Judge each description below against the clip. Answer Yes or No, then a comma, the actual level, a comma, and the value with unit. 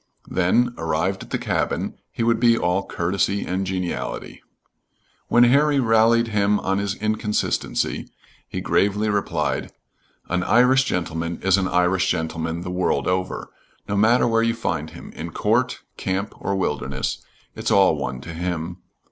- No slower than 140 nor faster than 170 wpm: Yes, average, 150 wpm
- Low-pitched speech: Yes, very low, 95 Hz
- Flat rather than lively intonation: No, average, 4.1 semitones